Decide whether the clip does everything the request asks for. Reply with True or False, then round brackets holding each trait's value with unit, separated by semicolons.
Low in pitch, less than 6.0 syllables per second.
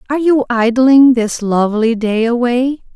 False (240 Hz; 4.6 syllables/s)